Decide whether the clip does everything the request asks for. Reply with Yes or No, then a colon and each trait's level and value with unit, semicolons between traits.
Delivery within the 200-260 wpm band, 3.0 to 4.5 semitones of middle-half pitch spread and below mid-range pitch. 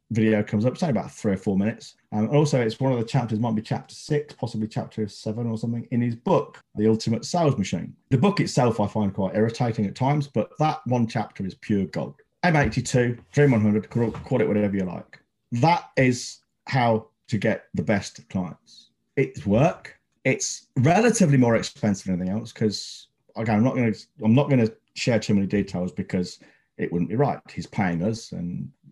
Yes: fast, 205 wpm; average, 3.5 semitones; low, 115 Hz